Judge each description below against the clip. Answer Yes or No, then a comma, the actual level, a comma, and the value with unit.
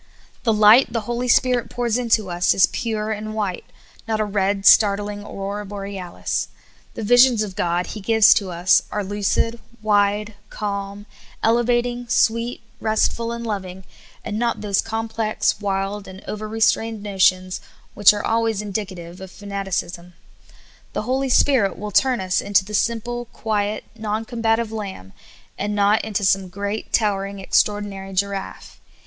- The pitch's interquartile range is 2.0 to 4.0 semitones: Yes, narrow, 2.4 semitones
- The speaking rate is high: No, average, 145 wpm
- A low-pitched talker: No, high, 210 Hz